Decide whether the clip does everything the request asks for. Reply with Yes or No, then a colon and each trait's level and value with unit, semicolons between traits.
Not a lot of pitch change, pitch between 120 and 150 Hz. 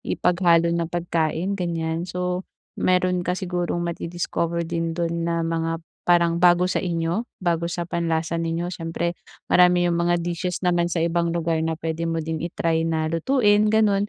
No: narrow, 1.4 semitones; medium, 170 Hz